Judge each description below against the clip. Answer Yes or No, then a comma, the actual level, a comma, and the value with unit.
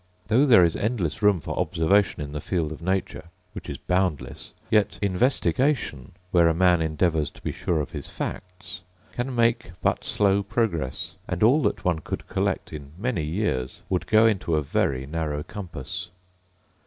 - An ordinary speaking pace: Yes, average, 170 wpm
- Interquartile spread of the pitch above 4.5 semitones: Yes, average, 5.0 semitones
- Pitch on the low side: Yes, very low, 90 Hz